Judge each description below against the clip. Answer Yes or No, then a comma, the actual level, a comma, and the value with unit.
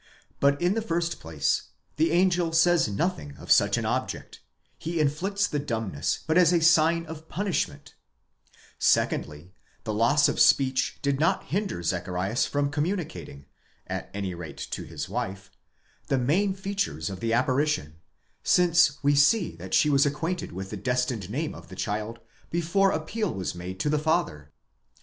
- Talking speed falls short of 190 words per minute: Yes, average, 165 wpm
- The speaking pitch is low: No, medium, 145 Hz